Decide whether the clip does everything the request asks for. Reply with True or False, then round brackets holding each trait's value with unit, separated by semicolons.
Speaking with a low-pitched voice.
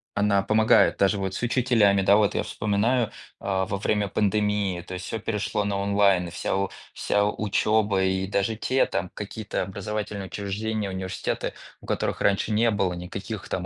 True (100 Hz)